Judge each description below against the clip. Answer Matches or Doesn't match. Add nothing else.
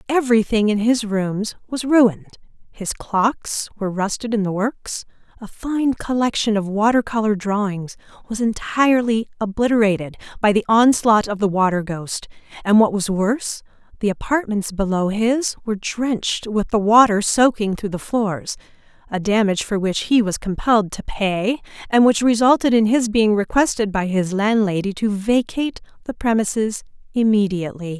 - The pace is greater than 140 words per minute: Matches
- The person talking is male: Doesn't match